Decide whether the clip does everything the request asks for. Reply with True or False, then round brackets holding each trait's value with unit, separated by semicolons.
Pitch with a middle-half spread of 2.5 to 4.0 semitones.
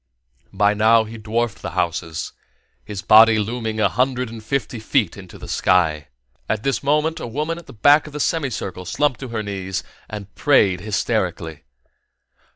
False (4.7 semitones)